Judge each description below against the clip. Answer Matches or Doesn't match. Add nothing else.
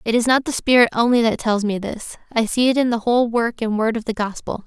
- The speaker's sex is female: Matches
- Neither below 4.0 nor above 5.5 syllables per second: Doesn't match